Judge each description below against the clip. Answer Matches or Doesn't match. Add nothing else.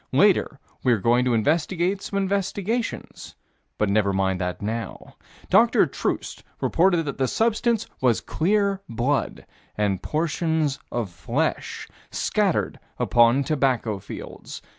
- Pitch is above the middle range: Doesn't match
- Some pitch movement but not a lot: Doesn't match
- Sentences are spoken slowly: Matches